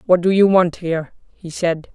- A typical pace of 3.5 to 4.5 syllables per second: No, 4.9 syllables/s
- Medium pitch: Yes, medium, 175 Hz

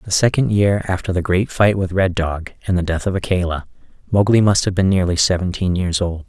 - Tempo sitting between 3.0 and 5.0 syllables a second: No, 5.5 syllables/s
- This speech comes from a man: Yes, male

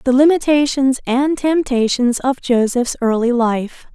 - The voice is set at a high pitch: Yes, very high, 255 Hz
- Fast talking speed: No, slow, 120 wpm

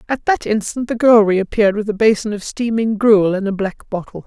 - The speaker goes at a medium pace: No, fast, 225 wpm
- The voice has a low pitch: No, high, 215 Hz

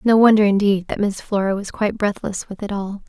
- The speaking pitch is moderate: No, high, 205 Hz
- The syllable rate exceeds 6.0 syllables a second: No, 5.7 syllables/s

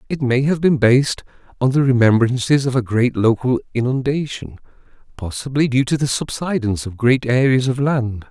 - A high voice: No, low, 125 Hz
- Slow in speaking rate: No, average, 165 wpm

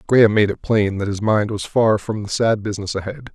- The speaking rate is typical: No, fast, 250 wpm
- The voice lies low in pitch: Yes, low, 105 Hz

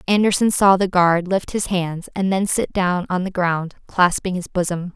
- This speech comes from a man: No, female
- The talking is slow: No, fast, 205 wpm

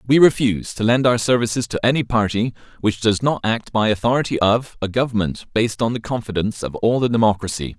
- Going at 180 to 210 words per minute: Yes, average, 200 wpm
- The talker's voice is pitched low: Yes, low, 110 Hz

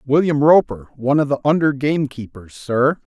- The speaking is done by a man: Yes, male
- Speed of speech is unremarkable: Yes, average, 150 wpm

